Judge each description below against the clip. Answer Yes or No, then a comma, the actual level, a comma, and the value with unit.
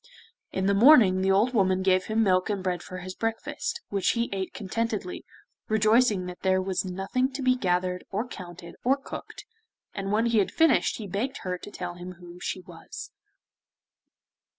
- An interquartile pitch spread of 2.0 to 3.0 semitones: No, average, 3.6 semitones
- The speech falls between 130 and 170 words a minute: No, average, 180 wpm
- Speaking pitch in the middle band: No, high, 195 Hz